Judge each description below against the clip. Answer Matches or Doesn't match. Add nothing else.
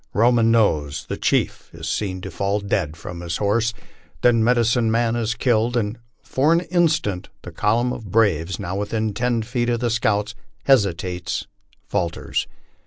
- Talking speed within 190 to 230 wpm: Doesn't match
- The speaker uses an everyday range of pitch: Matches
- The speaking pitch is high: Doesn't match